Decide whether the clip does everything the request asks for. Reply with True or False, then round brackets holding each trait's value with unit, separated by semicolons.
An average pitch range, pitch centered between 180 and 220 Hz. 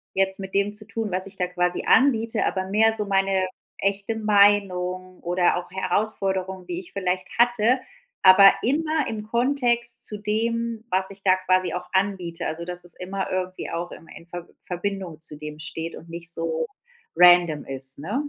True (3.1 semitones; 190 Hz)